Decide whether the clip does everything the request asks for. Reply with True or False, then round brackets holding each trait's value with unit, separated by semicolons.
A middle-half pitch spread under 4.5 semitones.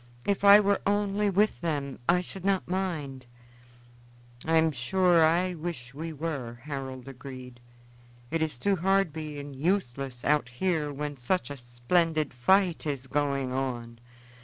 False (5.4 semitones)